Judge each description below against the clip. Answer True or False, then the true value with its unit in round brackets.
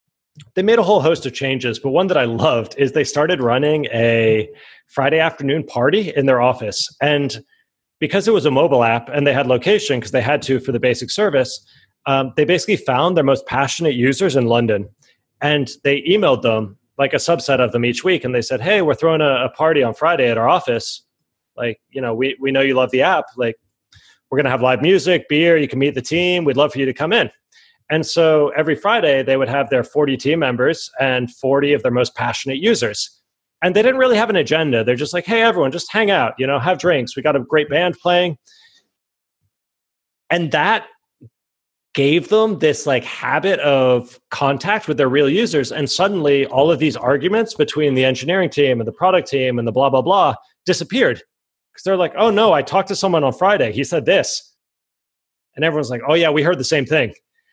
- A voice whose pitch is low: False (145 Hz)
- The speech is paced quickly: True (215 wpm)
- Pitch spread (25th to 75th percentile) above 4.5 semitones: True (5.1 semitones)